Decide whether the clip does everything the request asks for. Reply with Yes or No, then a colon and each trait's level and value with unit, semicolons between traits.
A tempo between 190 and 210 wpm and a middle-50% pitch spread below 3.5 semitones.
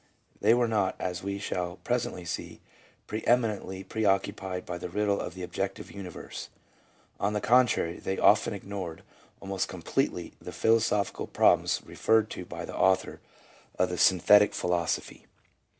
No: average, 150 wpm; average, 2.7 semitones